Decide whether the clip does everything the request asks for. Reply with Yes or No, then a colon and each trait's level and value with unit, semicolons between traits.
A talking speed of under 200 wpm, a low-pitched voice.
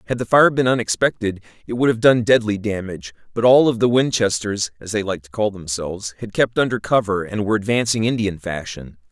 No: fast, 205 wpm; low, 105 Hz